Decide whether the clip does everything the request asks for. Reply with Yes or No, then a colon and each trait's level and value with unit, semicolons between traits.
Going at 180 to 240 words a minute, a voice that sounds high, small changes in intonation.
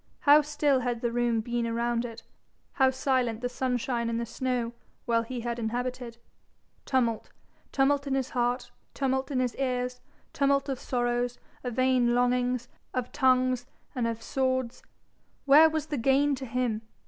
No: average, 160 wpm; very high, 250 Hz; narrow, 1.8 semitones